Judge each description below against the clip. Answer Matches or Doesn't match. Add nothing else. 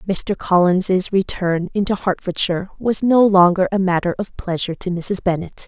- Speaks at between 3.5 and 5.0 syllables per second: Matches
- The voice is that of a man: Doesn't match